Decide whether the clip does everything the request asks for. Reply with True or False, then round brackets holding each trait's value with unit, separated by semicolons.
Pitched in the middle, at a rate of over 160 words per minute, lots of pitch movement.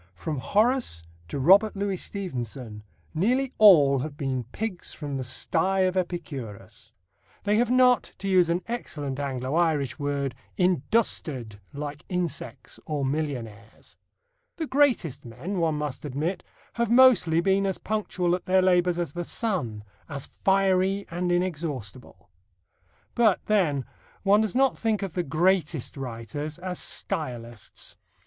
False (170 Hz; 135 wpm; 6.0 semitones)